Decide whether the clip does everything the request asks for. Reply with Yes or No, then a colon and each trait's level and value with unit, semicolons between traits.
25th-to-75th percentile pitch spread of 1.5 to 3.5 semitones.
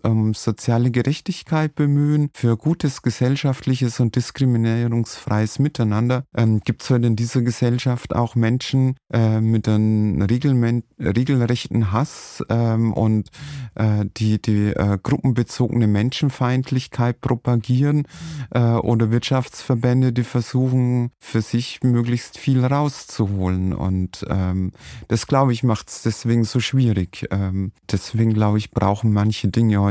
Yes: average, 2.9 semitones